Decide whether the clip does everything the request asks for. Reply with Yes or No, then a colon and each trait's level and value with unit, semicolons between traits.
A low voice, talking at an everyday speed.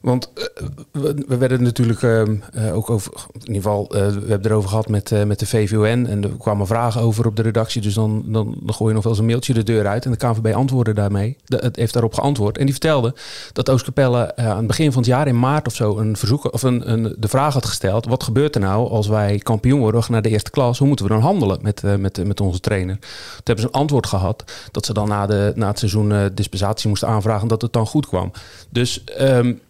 No: low, 115 Hz; fast, 255 wpm